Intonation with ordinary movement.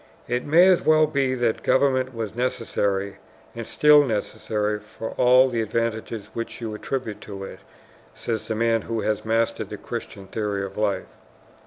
Yes: average, 3.2 semitones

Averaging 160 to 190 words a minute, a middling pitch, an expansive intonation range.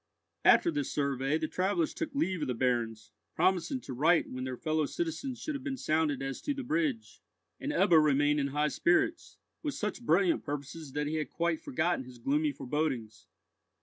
Yes: average, 185 wpm; medium, 155 Hz; wide, 6.7 semitones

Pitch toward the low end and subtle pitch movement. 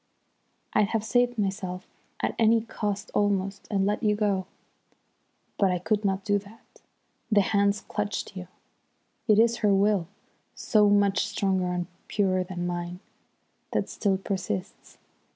No: high, 200 Hz; narrow, 1.9 semitones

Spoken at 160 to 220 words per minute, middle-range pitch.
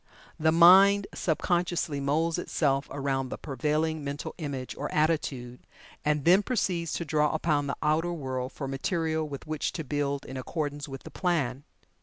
Yes: average, 165 wpm; medium, 150 Hz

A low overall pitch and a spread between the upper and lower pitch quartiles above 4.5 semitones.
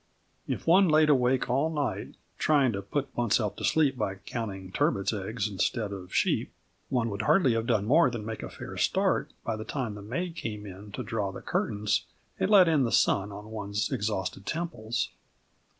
Yes: low, 115 Hz; average, 5.0 semitones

